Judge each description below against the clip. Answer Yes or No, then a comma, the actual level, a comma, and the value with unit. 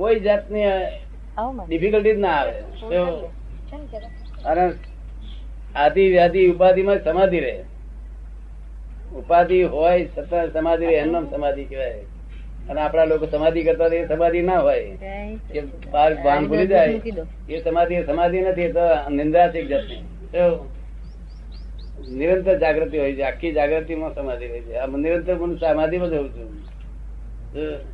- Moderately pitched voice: Yes, medium, 160 Hz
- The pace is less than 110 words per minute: Yes, average, 85 wpm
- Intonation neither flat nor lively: Yes, average, 4.7 semitones